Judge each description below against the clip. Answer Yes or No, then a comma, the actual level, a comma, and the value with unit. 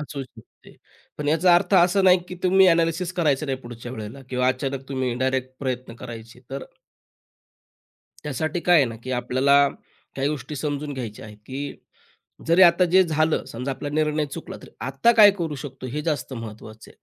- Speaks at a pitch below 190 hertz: Yes, medium, 140 Hz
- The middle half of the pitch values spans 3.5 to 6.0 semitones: Yes, average, 4.3 semitones